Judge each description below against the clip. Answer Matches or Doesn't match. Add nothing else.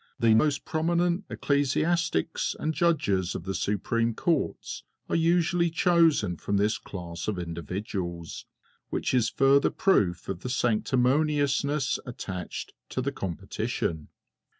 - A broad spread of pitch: Matches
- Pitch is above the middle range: Doesn't match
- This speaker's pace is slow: Matches